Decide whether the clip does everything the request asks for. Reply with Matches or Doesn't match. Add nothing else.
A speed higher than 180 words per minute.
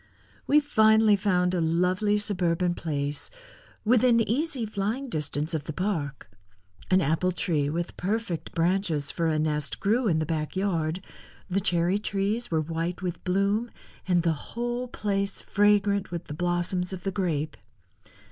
Doesn't match